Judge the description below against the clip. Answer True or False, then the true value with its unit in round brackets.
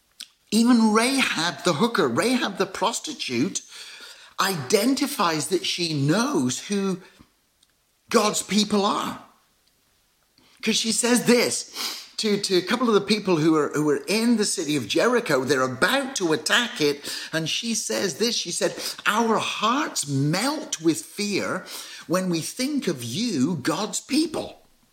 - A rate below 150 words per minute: True (140 wpm)